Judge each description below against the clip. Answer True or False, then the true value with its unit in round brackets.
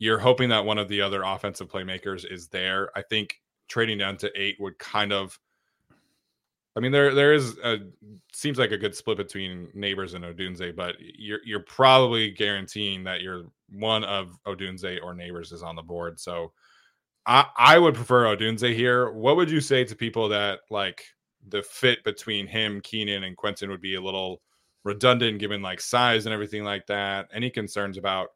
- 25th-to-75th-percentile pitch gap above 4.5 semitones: False (2.7 semitones)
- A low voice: True (100 Hz)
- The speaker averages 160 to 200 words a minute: True (185 wpm)